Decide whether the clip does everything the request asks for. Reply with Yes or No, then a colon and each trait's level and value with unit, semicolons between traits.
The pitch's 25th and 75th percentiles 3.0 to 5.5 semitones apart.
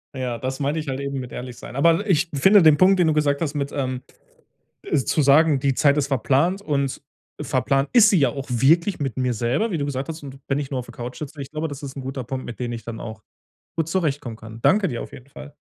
Yes: average, 3.4 semitones